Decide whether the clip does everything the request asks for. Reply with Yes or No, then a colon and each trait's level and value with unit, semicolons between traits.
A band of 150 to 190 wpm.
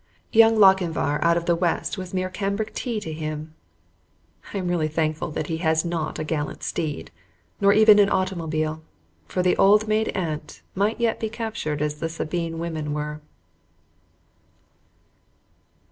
Yes: average, 155 wpm